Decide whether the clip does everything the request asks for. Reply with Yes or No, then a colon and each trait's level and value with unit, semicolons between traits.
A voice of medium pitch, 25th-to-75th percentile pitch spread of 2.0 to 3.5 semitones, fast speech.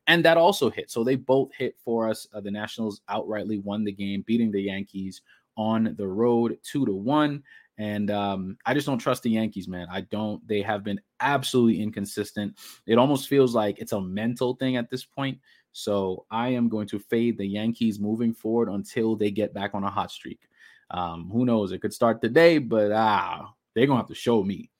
No: low, 110 Hz; average, 2.7 semitones; fast, 210 wpm